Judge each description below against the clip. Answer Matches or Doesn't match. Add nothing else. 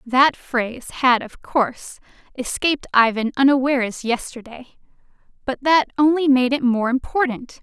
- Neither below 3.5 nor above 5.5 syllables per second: Matches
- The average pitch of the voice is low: Doesn't match